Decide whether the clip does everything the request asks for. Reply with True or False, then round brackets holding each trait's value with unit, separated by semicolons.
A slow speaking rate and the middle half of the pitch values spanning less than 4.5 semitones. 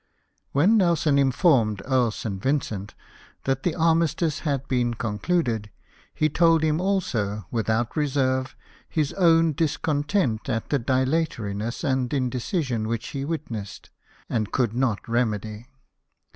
False (125 wpm; 5.6 semitones)